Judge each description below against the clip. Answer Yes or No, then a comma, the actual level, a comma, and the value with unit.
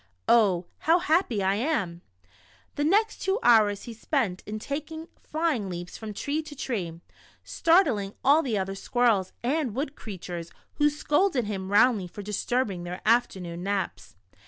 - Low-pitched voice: No, high, 225 Hz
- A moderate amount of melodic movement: No, wide, 7.4 semitones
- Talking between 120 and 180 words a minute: Yes, average, 150 wpm